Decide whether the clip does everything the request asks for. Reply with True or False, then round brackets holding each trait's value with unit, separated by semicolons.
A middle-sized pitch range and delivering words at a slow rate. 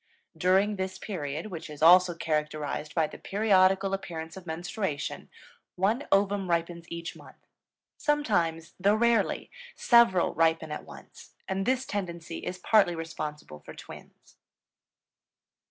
True (3.4 semitones; 125 wpm)